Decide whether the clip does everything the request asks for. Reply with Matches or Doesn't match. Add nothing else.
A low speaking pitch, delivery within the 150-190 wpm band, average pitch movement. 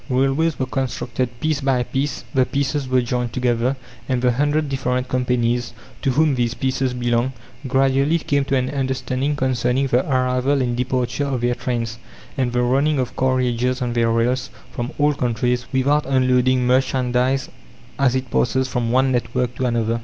Doesn't match